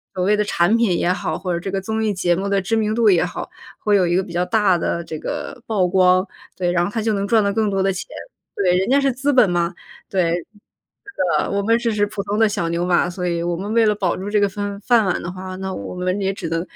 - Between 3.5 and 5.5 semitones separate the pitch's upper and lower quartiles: No, average, 2.9 semitones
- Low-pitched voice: No, high, 195 Hz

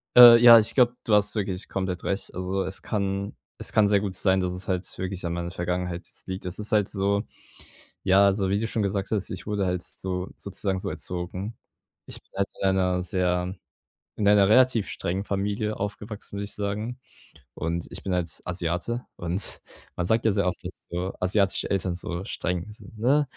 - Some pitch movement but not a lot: No, narrow, 2.3 semitones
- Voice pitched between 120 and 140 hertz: No, very low, 95 Hz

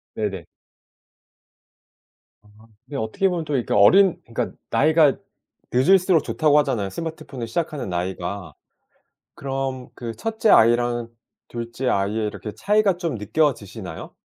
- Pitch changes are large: Yes, wide, 6.7 semitones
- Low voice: Yes, low, 130 Hz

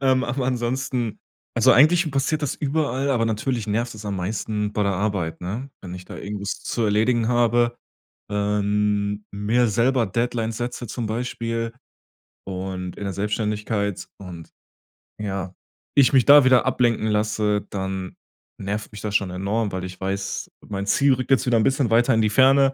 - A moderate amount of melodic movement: Yes, average, 3.5 semitones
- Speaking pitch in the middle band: No, low, 110 Hz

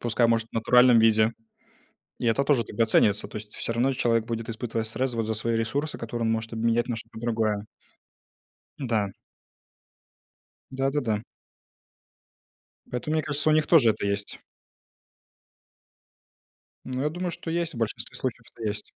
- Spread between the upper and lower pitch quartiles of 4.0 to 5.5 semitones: No, average, 2.8 semitones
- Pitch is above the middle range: No, low, 115 Hz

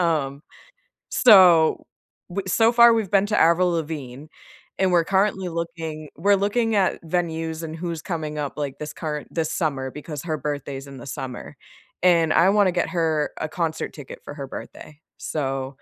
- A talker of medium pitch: Yes, medium, 160 Hz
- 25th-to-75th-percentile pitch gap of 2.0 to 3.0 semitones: No, average, 3.5 semitones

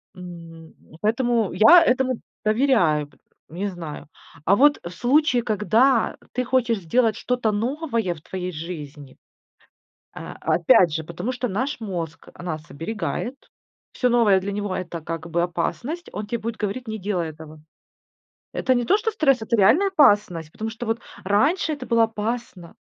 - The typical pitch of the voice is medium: No, high, 215 Hz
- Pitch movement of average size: No, wide, 6.3 semitones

